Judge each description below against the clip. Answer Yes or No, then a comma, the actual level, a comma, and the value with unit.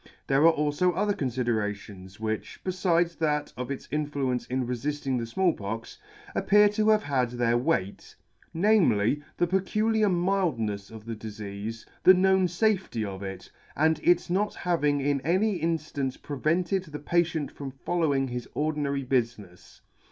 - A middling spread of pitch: No, wide, 6.8 semitones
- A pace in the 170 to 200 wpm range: No, average, 145 wpm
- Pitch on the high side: No, medium, 145 Hz